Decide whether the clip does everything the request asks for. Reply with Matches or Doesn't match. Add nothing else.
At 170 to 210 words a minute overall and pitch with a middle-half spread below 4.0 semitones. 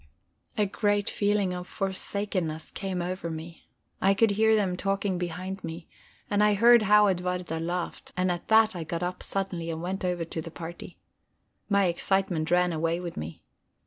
Matches